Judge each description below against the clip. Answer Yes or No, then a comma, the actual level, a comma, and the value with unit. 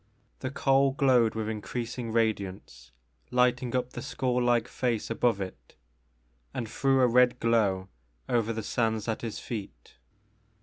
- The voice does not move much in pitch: Yes, narrow, 2.3 semitones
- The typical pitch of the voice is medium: No, low, 115 Hz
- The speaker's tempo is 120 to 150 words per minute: Yes, average, 140 wpm